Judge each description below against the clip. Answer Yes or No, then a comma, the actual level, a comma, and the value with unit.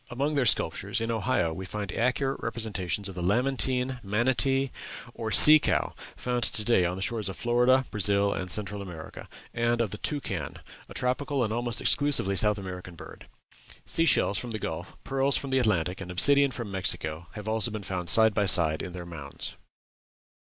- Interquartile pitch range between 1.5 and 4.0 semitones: No, average, 5.1 semitones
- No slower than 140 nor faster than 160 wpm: No, average, 185 wpm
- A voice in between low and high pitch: No, low, 110 Hz